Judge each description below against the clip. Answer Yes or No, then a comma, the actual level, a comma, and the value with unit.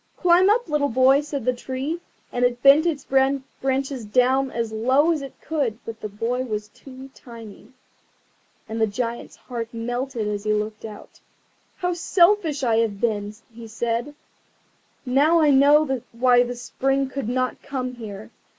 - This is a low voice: No, very high, 255 Hz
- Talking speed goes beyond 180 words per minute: No, average, 160 wpm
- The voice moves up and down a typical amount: Yes, average, 3.4 semitones